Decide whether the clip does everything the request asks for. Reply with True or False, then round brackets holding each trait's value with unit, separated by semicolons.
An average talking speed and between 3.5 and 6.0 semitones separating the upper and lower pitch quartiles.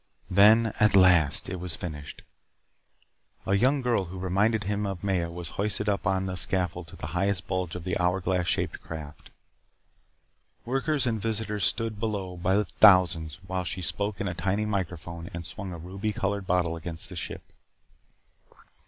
False (170 wpm; 2.8 semitones)